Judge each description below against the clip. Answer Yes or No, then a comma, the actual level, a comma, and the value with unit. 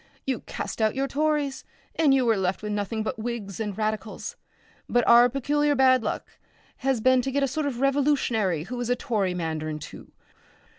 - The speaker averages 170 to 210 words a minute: Yes, average, 190 wpm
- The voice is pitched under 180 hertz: No, high, 240 Hz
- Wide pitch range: No, average, 4.4 semitones